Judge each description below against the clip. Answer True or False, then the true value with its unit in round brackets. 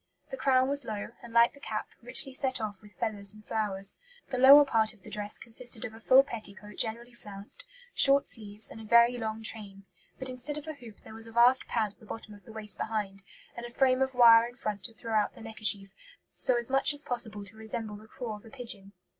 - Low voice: False (225 Hz)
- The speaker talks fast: True (240 wpm)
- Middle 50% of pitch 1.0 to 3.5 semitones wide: True (2.8 semitones)